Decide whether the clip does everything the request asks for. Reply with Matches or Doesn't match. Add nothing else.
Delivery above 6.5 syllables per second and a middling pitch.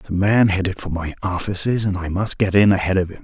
Doesn't match